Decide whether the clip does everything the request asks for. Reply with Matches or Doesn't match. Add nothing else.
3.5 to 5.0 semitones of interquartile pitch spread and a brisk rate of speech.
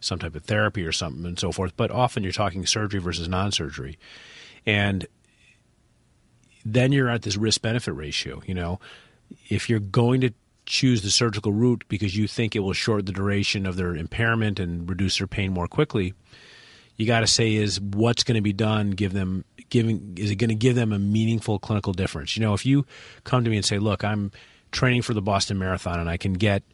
Doesn't match